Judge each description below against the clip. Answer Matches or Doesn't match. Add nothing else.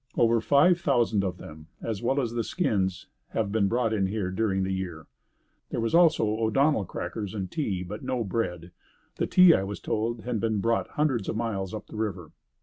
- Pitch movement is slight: Doesn't match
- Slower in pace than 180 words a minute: Doesn't match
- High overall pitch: Doesn't match